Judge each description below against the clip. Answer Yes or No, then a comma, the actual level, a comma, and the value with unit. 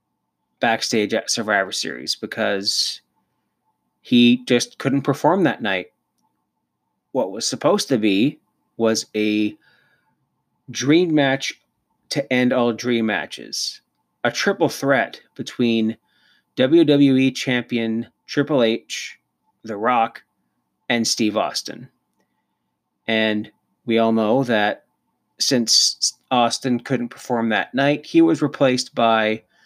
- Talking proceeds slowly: Yes, slow, 105 wpm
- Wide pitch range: No, average, 3.2 semitones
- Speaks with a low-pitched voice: Yes, low, 120 Hz